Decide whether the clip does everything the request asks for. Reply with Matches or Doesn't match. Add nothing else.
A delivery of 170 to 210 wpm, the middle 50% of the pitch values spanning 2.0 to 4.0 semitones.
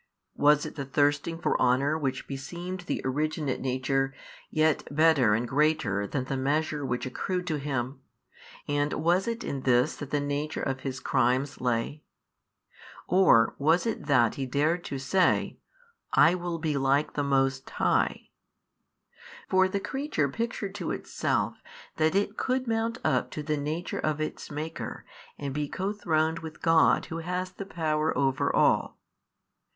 Doesn't match